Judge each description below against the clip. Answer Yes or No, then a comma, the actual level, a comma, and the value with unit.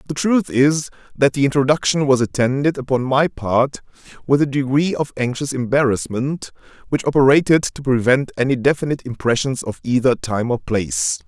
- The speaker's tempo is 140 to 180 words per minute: Yes, average, 150 wpm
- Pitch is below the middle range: Yes, low, 130 Hz